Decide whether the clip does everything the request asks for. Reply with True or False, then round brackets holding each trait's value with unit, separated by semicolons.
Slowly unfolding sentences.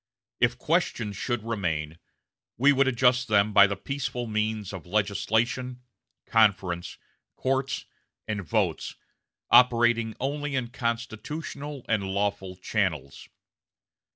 True (105 wpm)